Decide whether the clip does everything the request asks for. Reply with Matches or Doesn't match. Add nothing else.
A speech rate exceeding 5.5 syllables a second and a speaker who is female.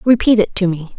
Matches